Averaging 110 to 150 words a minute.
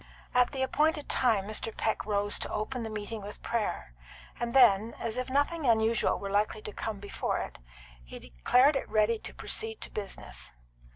No: average, 175 wpm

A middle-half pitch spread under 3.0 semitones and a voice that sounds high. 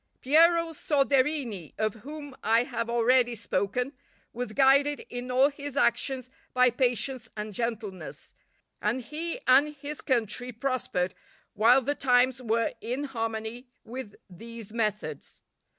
No: average, 3.4 semitones; very high, 250 Hz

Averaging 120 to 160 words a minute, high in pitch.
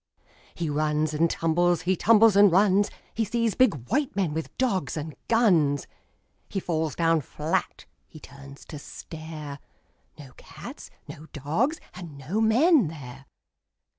No: average, 145 wpm; medium, 165 Hz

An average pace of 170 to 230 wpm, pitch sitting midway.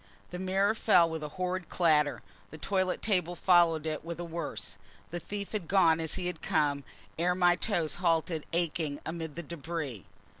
Yes: average, 180 wpm; medium, 170 Hz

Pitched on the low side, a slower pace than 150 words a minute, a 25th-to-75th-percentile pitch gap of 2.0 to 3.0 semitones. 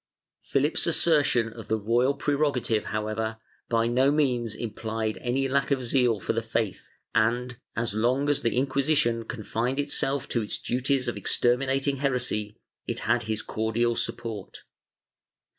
No: low, 120 Hz; average, 140 wpm; average, 3.4 semitones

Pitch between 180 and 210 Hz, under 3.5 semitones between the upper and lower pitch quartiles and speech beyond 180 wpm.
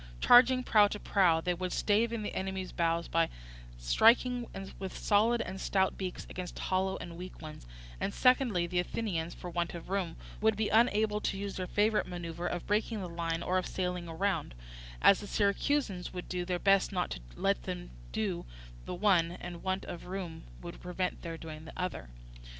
Yes: medium, 185 Hz; average, 3.1 semitones; average, 190 wpm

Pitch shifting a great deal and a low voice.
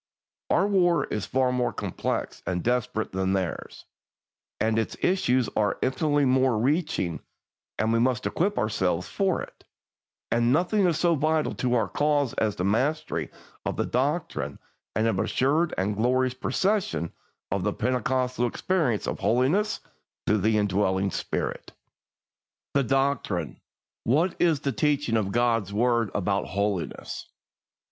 Yes: wide, 5.8 semitones; low, 125 Hz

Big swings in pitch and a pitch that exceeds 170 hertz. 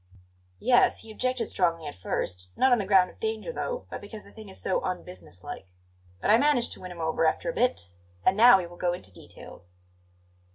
Yes: wide, 6.5 semitones; high, 190 Hz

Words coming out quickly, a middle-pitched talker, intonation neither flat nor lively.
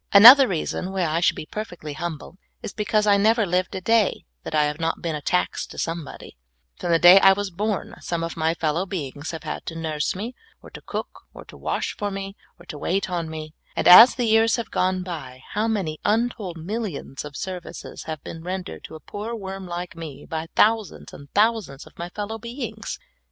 Yes: fast, 215 wpm; medium, 180 Hz; average, 4.3 semitones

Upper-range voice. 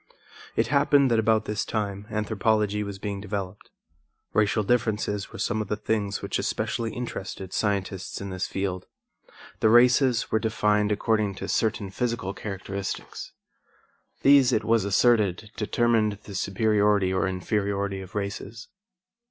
No: low, 105 Hz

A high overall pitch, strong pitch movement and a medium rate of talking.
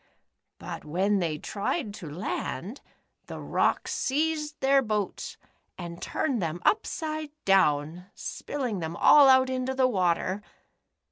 No: high, 210 Hz; wide, 7.5 semitones; slow, 125 wpm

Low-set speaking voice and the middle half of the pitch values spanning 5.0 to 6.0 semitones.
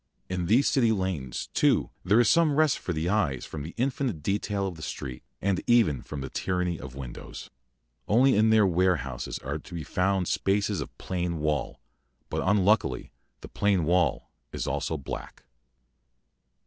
Yes: very low, 90 Hz; average, 5.3 semitones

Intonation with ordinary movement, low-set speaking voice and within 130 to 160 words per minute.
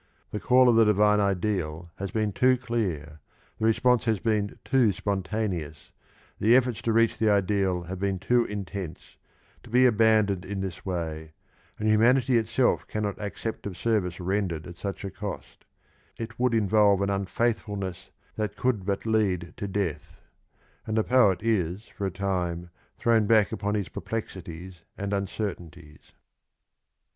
Yes: average, 3.3 semitones; low, 100 Hz; average, 155 wpm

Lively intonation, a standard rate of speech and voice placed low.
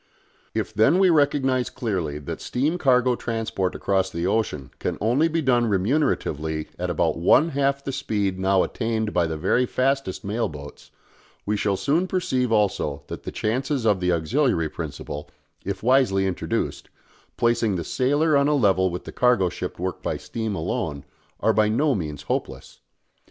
Yes: wide, 6.4 semitones; average, 165 wpm; low, 110 Hz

